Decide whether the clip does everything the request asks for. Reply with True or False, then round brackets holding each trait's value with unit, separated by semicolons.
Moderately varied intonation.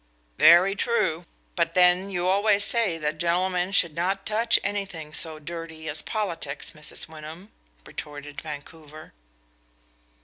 True (3.8 semitones)